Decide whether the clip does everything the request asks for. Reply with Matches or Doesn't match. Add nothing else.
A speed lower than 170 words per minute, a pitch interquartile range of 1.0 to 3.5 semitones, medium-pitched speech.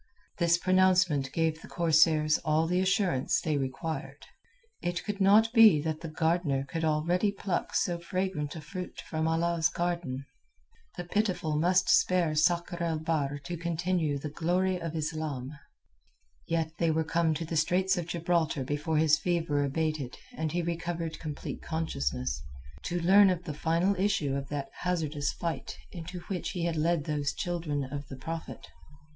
Matches